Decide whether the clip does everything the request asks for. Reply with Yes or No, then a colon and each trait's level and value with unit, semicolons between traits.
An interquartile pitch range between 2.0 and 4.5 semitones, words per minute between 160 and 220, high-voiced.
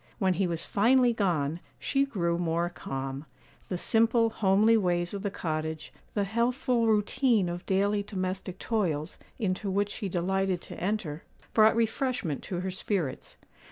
No: average, 4.1 semitones; average, 150 wpm; high, 195 Hz